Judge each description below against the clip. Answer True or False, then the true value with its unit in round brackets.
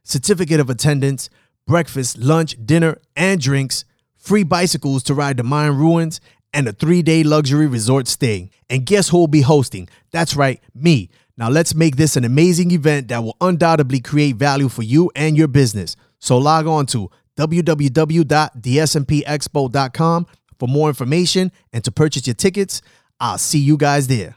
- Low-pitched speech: False (150 Hz)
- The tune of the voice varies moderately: True (3.9 semitones)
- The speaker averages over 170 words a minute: False (165 wpm)